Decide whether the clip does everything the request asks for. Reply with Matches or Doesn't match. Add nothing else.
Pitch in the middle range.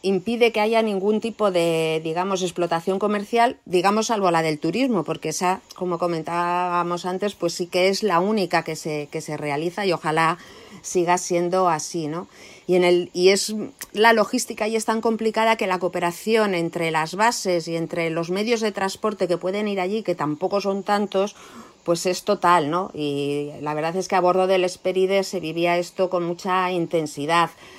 Matches